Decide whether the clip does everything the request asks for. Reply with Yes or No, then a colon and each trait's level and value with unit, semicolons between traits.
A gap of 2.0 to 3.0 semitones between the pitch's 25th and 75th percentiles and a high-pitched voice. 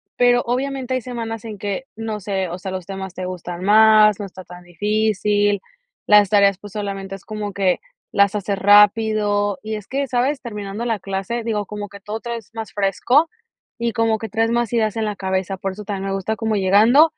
Yes: narrow, 2.5 semitones; high, 210 Hz